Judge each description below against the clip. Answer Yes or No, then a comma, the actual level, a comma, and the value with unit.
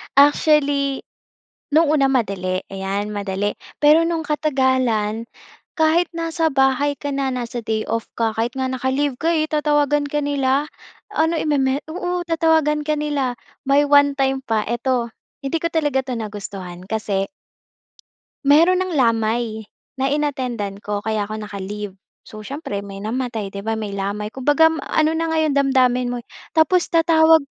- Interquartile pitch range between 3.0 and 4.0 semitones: No, wide, 5.5 semitones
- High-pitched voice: Yes, very high, 265 Hz